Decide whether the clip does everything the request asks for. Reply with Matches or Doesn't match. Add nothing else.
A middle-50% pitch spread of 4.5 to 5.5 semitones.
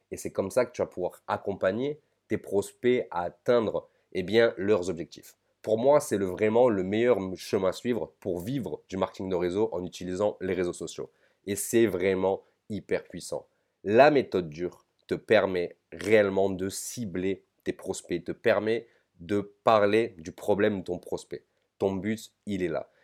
Doesn't match